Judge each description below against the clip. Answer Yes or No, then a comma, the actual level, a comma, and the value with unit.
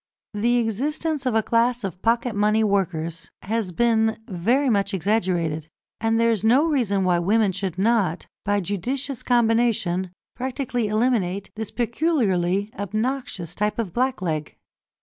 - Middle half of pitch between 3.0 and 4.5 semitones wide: Yes, average, 4.1 semitones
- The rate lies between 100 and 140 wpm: Yes, slow, 135 wpm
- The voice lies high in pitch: Yes, high, 220 Hz